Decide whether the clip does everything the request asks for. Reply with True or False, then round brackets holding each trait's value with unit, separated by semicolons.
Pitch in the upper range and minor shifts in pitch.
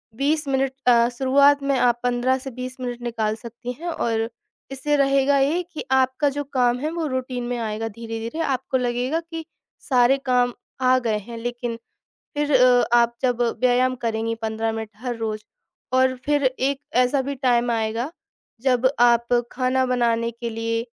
True (250 Hz; 2.3 semitones)